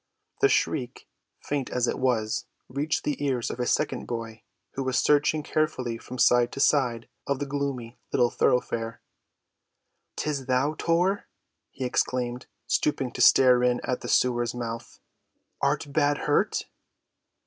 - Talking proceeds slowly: No, average, 145 wpm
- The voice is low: Yes, low, 130 Hz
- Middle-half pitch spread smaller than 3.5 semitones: Yes, average, 2.9 semitones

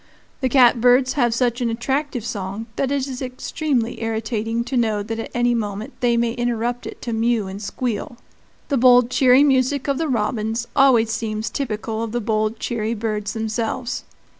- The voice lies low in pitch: No, high, 235 Hz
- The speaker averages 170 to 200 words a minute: Yes, average, 175 wpm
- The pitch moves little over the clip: Yes, narrow, 2.3 semitones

